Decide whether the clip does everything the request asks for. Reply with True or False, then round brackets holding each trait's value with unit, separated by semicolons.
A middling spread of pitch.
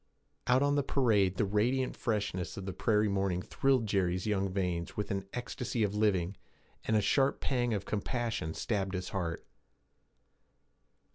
True (3.9 semitones)